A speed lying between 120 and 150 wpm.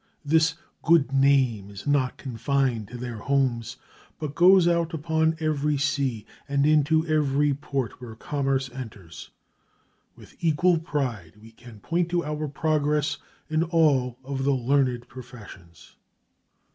Yes: slow, 135 wpm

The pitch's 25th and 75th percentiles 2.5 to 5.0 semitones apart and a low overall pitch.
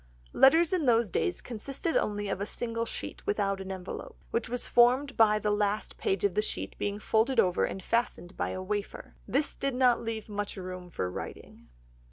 No: average, 3.7 semitones; high, 215 Hz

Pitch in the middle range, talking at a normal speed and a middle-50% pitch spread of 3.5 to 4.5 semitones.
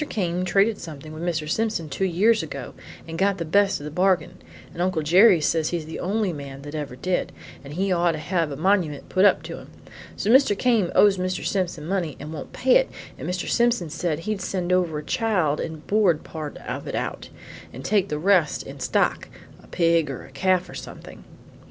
No: medium, 175 Hz; fast, 215 wpm; average, 4.0 semitones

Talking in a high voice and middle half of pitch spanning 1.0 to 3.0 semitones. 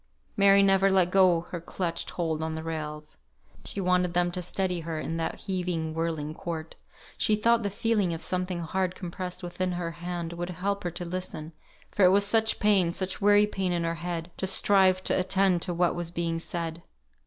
No: medium, 180 Hz; narrow, 2.4 semitones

